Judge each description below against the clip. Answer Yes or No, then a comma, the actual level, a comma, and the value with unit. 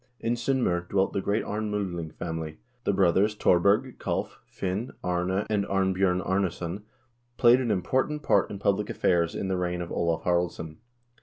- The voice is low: Yes, very low, 95 Hz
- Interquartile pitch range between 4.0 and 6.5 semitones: No, average, 2.9 semitones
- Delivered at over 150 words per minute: Yes, average, 160 wpm